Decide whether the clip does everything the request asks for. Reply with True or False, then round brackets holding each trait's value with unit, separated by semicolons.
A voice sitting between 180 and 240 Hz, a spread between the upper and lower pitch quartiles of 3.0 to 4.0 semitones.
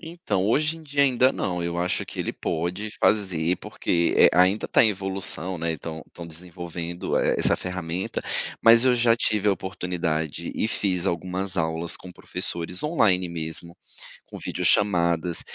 False (90 Hz; 3.4 semitones)